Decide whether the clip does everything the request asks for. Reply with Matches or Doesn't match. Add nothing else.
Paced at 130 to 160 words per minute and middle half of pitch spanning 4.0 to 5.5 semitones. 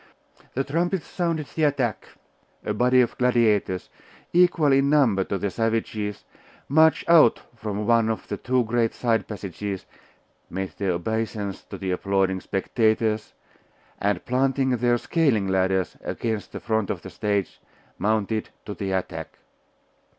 Matches